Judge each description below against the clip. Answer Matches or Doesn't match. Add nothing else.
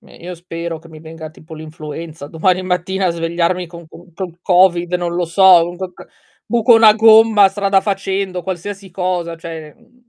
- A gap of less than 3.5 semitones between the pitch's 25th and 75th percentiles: Matches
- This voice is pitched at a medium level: Matches